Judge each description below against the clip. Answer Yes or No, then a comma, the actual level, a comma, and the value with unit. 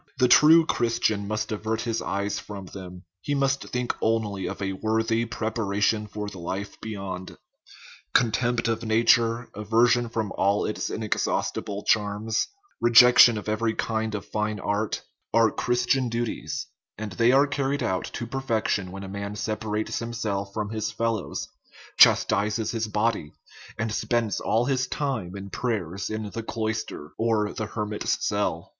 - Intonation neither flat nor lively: No, narrow, 2.3 semitones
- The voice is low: Yes, low, 110 Hz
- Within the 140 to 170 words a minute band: Yes, average, 155 wpm